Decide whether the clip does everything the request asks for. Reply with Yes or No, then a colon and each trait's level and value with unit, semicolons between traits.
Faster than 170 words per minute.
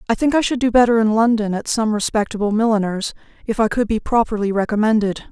Yes: fast, 205 wpm